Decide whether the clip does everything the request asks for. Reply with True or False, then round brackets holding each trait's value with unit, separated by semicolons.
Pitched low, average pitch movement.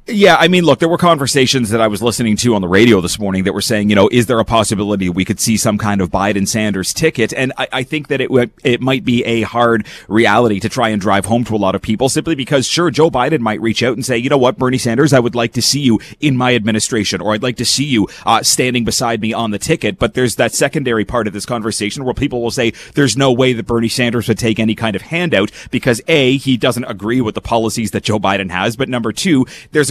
True (120 Hz; 3.2 semitones)